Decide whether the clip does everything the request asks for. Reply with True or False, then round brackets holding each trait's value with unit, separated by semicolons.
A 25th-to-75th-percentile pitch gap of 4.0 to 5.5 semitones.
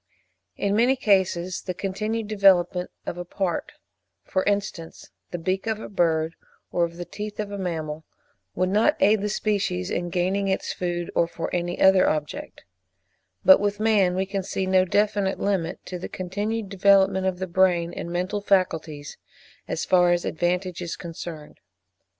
False (2.6 semitones)